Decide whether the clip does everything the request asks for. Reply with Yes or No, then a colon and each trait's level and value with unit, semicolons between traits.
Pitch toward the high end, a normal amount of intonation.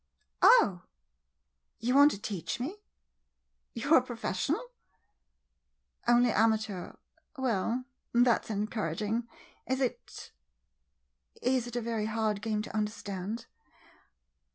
Yes: high, 225 Hz; average, 3.2 semitones